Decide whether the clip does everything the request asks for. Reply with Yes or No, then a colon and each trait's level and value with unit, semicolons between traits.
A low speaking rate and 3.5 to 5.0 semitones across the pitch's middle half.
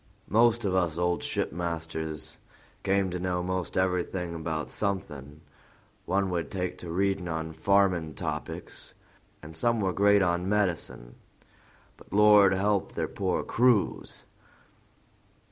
No: slow, 125 wpm; average, 3.1 semitones